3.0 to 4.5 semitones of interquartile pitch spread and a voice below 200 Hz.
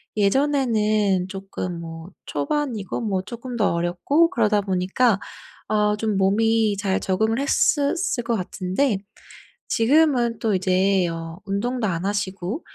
No: average, 3.9 semitones; high, 210 Hz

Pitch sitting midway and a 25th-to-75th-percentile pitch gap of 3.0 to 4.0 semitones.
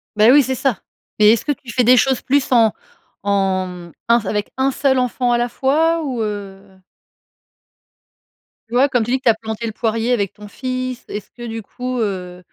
No: high, 235 Hz; average, 3.6 semitones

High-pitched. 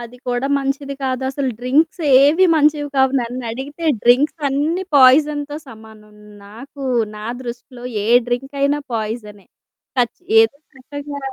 Yes: very high, 270 Hz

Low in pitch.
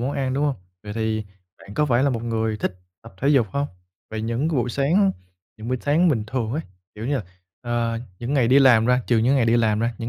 Yes: low, 120 Hz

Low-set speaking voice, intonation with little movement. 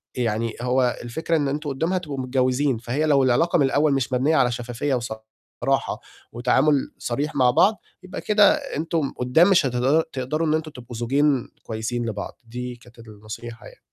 No: low, 130 Hz; average, 4.1 semitones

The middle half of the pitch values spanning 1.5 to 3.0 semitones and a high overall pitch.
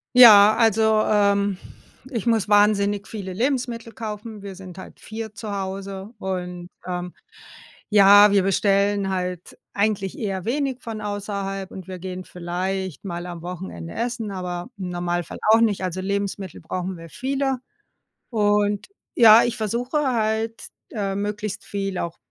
Yes: average, 2.7 semitones; high, 200 Hz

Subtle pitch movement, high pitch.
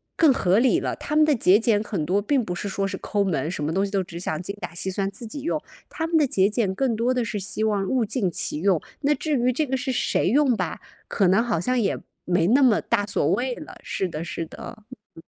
No: average, 5.3 semitones; high, 210 Hz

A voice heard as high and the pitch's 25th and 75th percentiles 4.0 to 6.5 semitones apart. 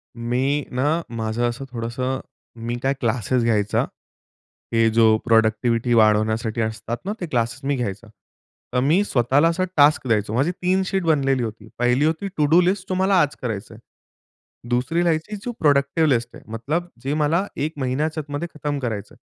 No: low, 130 Hz; average, 5.2 semitones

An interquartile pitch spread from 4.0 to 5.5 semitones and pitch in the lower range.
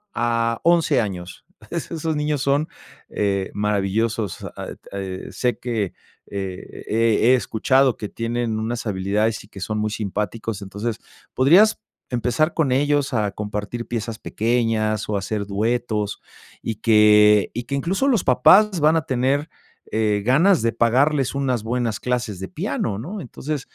Yes: average, 4.3 semitones; low, 115 Hz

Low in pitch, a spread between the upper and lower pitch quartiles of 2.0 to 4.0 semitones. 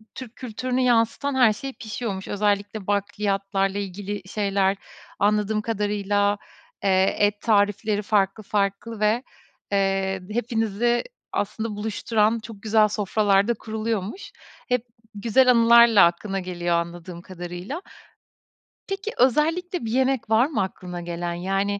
No: high, 210 Hz; average, 2.8 semitones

